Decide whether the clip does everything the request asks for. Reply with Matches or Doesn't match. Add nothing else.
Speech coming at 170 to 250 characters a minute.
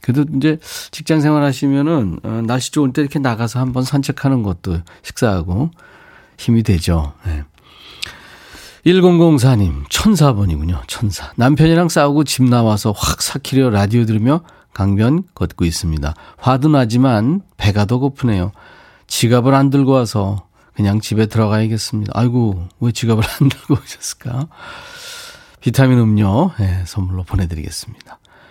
Doesn't match